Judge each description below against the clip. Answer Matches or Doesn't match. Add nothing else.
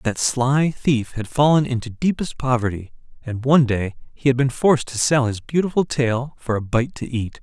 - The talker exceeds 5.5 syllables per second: Doesn't match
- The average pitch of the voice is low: Matches